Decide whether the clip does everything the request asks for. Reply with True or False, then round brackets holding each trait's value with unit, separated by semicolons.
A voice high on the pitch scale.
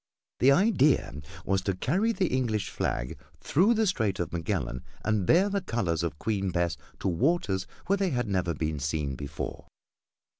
False (100 Hz)